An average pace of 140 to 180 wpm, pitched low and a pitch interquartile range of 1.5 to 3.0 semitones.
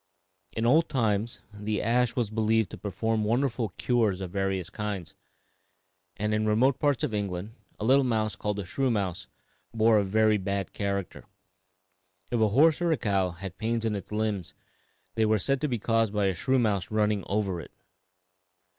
Yes: average, 175 wpm; low, 110 Hz; average, 2.7 semitones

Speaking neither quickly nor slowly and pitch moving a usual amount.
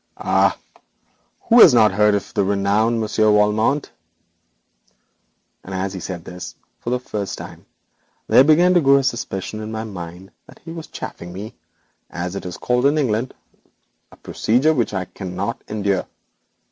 Yes: average, 160 wpm; average, 4.5 semitones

